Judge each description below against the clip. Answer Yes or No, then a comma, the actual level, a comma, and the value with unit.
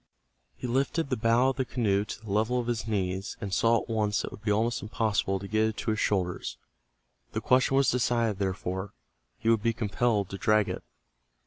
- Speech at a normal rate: No, fast, 215 wpm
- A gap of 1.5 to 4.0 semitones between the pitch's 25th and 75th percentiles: Yes, average, 2.8 semitones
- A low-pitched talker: Yes, low, 110 Hz